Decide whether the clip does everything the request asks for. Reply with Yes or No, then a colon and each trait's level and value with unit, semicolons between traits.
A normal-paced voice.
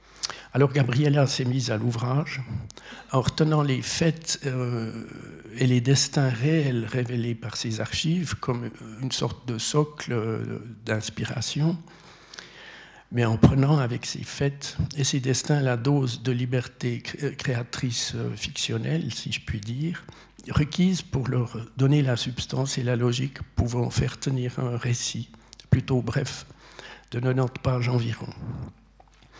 No: slow, 130 wpm